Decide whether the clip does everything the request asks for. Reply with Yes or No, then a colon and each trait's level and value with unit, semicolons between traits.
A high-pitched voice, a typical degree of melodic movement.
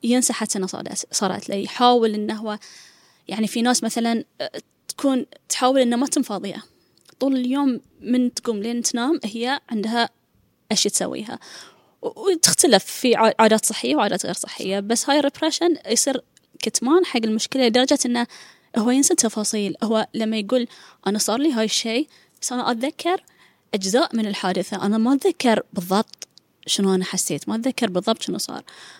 Yes: high, 235 Hz; average, 3.5 semitones